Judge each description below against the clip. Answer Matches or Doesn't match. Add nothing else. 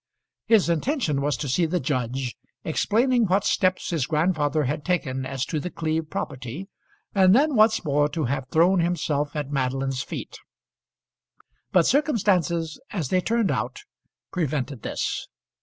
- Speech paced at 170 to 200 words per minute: Doesn't match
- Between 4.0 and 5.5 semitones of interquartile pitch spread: Matches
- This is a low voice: Doesn't match